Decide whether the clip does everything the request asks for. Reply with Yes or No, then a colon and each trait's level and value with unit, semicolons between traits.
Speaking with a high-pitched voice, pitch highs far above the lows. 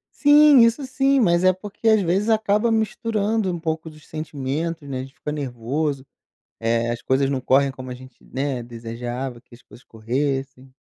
No: medium, 145 Hz; wide, 7.8 semitones